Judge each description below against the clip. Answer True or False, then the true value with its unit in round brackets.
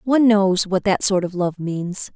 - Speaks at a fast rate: True (220 wpm)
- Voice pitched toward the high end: True (195 Hz)